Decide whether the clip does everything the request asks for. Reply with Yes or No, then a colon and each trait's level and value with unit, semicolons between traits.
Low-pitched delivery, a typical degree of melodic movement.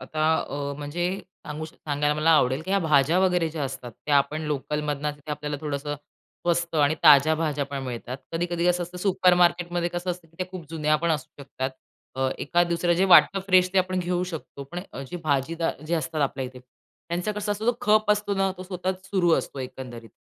No: medium, 165 Hz; average, 3.6 semitones